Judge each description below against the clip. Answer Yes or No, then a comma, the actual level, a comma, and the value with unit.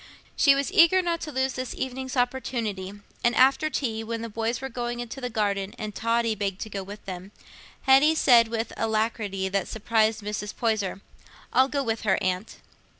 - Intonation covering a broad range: No, average, 3.9 semitones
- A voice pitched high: Yes, high, 230 Hz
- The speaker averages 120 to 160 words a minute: No, average, 190 wpm